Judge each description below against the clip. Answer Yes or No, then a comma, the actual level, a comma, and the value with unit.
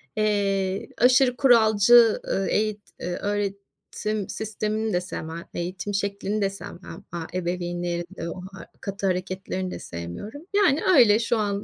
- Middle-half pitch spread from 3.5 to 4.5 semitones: No, average, 2.9 semitones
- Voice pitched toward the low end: No, high, 200 Hz